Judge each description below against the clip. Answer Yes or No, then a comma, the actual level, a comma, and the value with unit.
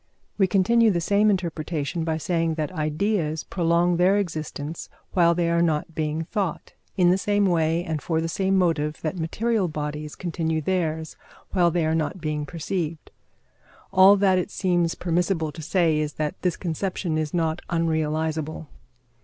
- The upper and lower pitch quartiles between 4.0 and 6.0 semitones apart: No, average, 2.7 semitones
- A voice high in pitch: No, medium, 165 Hz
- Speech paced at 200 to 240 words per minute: No, average, 160 wpm